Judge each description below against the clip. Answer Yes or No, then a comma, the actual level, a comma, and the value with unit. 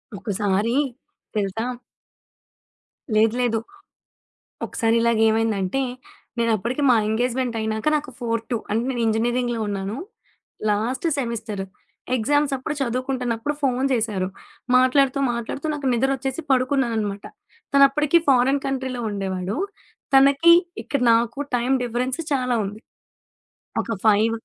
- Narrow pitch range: No, average, 3.3 semitones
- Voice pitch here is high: Yes, high, 235 Hz